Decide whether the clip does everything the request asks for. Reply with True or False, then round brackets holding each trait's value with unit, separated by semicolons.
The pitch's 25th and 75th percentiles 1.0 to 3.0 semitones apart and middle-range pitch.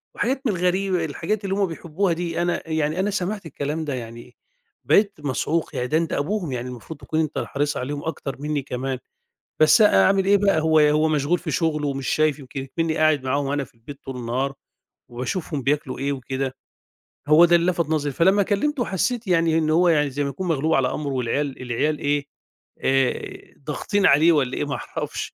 False (3.9 semitones; 155 Hz)